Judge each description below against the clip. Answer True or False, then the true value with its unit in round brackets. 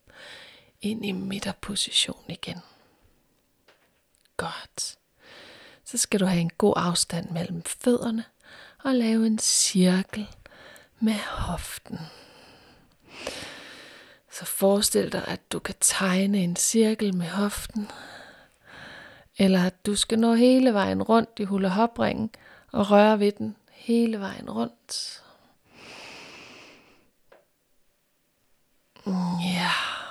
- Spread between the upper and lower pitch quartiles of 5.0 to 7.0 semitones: False (3.2 semitones)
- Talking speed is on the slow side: True (105 wpm)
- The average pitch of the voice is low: False (210 Hz)